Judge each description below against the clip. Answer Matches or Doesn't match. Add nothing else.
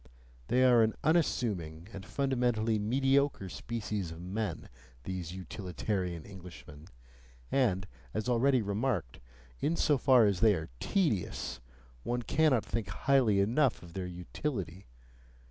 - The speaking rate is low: Matches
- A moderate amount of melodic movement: Doesn't match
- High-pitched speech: Doesn't match